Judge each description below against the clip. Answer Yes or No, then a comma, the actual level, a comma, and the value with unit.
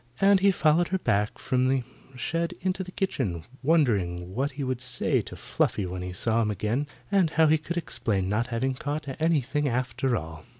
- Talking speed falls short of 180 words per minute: No, average, 195 wpm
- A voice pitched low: Yes, low, 130 Hz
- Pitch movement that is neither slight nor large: No, wide, 7.2 semitones